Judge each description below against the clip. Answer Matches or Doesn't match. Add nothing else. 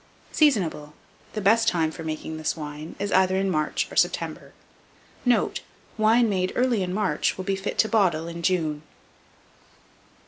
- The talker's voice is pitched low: Doesn't match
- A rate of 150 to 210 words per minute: Matches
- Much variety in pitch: Doesn't match